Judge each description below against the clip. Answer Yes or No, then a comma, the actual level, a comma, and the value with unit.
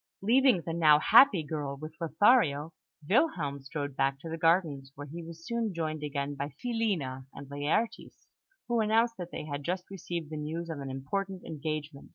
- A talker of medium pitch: Yes, medium, 160 Hz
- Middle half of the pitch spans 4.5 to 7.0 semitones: Yes, average, 5.1 semitones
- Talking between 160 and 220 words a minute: Yes, average, 180 wpm